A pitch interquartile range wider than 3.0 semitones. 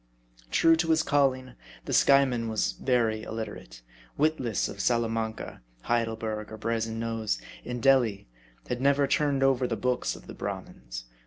Yes: average, 3.4 semitones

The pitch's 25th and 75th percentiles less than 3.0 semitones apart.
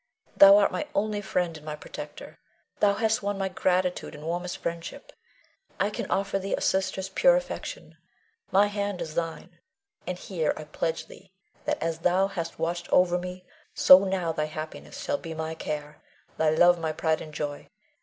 No: average, 3.5 semitones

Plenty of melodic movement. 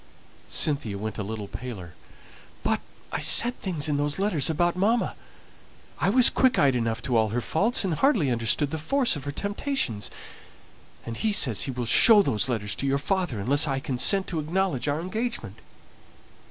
Yes: wide, 8.4 semitones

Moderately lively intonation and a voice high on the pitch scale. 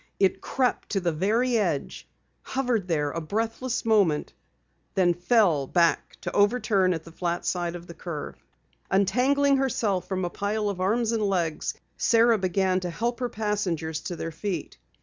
Yes: average, 4.6 semitones; high, 195 Hz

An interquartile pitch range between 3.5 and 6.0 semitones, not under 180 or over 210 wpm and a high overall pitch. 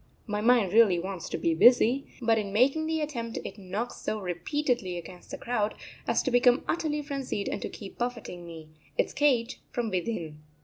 Yes: average, 5.1 semitones; average, 185 wpm; high, 230 Hz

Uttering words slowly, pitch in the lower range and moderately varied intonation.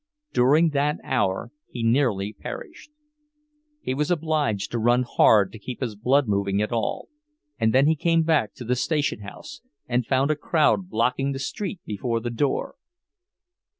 No: average, 160 wpm; low, 125 Hz; average, 4.9 semitones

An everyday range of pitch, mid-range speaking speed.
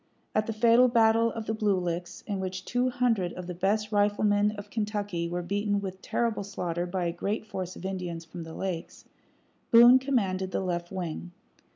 Yes: average, 3.4 semitones; average, 190 wpm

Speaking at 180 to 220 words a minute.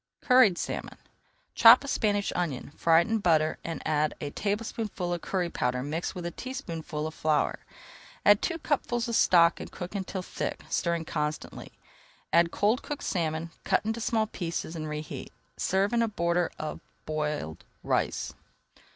No: average, 160 wpm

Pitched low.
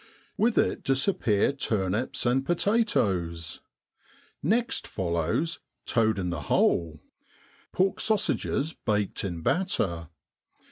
Yes: low, 110 Hz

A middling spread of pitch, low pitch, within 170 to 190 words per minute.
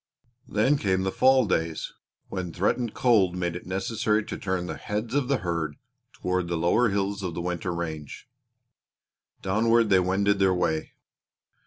No: average, 3.6 semitones; very low, 95 Hz; average, 160 wpm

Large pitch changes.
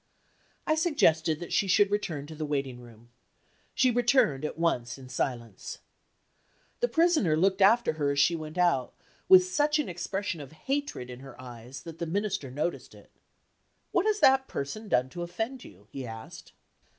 Yes: wide, 8.8 semitones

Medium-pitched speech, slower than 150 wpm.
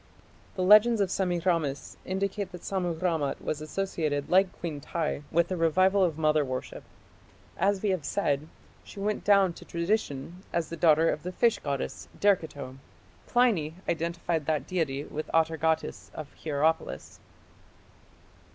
Yes: medium, 170 Hz; average, 140 wpm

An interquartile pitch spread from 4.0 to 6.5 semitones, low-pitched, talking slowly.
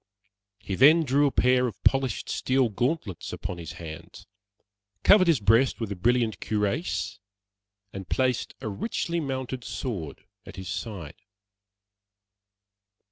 Yes: average, 5.3 semitones; low, 120 Hz; slow, 130 wpm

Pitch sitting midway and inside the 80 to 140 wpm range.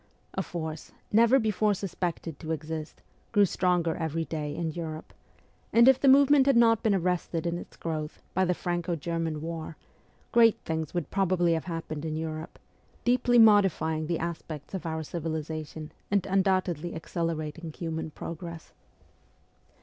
No: medium, 170 Hz; average, 150 wpm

